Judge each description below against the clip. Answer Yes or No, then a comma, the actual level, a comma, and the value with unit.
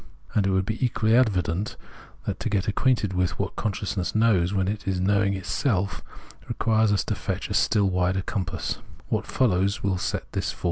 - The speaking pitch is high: No, low, 100 Hz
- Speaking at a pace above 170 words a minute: No, average, 150 wpm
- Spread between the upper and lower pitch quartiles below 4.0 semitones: Yes, narrow, 2.5 semitones